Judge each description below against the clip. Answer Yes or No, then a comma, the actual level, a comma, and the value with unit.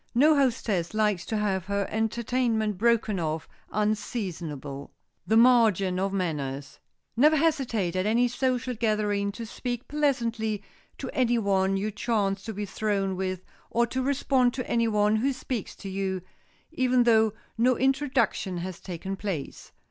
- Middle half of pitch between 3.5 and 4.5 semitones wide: Yes, average, 4.0 semitones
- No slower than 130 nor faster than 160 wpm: Yes, average, 150 wpm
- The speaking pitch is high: Yes, high, 215 Hz